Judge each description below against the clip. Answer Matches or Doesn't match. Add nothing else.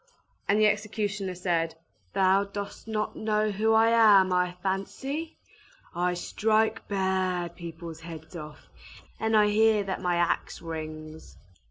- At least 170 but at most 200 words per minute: Doesn't match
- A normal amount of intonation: Matches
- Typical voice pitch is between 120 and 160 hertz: Doesn't match